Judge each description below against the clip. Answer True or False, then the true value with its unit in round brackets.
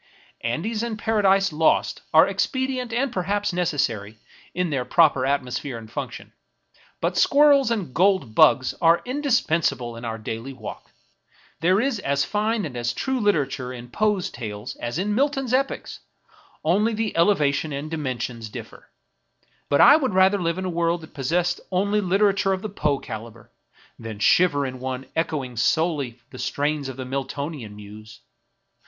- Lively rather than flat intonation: True (8.1 semitones)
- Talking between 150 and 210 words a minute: True (160 wpm)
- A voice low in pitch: False (160 Hz)